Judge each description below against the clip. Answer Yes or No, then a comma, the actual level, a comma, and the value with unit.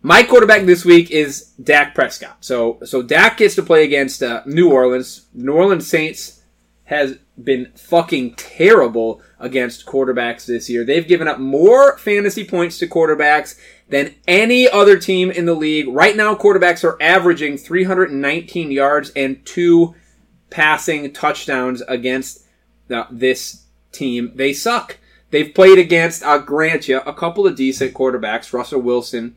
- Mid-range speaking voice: Yes, medium, 150 Hz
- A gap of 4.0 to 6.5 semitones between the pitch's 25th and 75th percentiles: Yes, average, 5.3 semitones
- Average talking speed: Yes, average, 150 wpm